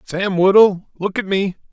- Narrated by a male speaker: Yes, male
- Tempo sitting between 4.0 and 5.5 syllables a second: Yes, 4.3 syllables/s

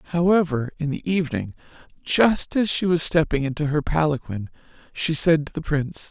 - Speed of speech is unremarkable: Yes, average, 165 wpm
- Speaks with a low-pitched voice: No, medium, 155 Hz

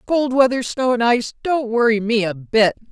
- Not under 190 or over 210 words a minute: Yes, fast, 205 wpm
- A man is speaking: No, female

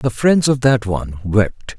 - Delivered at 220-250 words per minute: No, average, 200 wpm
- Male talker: Yes, male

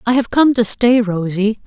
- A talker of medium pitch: No, high, 225 Hz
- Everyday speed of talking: No, fast, 215 wpm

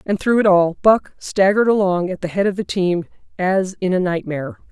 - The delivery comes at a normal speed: No, fast, 215 wpm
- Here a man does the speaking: No, female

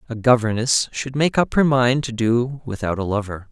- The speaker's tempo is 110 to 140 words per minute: No, fast, 205 wpm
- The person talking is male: Yes, male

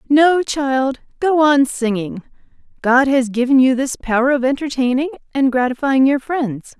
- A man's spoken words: No, female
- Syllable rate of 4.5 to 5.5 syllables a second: Yes, 4.6 syllables/s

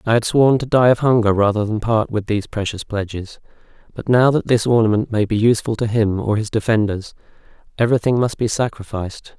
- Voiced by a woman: No, male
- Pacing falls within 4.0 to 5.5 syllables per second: No, 5.9 syllables/s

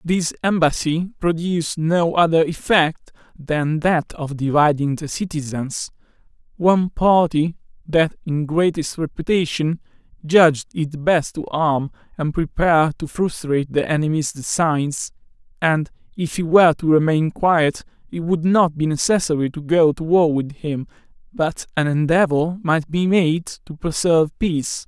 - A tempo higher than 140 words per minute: No, slow, 135 wpm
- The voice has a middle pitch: Yes, medium, 160 Hz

